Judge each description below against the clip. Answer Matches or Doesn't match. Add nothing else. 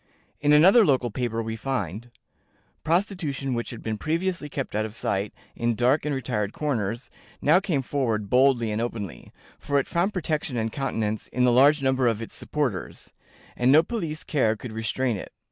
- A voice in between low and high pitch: Doesn't match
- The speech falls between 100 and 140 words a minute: Doesn't match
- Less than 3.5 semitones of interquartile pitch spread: Doesn't match